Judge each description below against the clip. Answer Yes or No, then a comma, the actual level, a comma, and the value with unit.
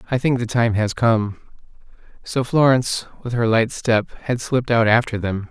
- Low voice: Yes, low, 115 Hz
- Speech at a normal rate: Yes, average, 185 wpm